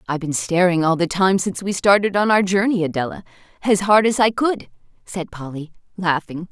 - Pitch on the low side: No, medium, 180 Hz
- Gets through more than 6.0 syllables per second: No, 5.6 syllables/s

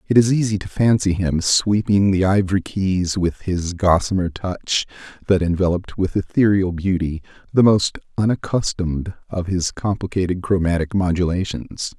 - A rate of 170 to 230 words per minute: No, slow, 135 wpm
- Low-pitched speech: Yes, very low, 95 Hz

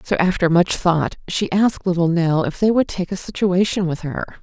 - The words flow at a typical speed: No, fast, 215 wpm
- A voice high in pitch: No, medium, 180 Hz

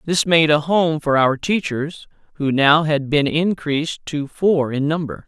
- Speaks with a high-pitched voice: No, medium, 155 Hz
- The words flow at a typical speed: Yes, average, 180 wpm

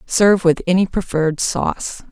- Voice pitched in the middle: Yes, medium, 180 Hz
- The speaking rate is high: No, average, 140 wpm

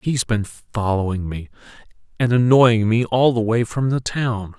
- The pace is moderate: Yes, average, 185 wpm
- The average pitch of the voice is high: No, low, 115 Hz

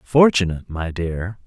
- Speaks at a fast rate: No, slow, 125 wpm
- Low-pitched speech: Yes, very low, 95 Hz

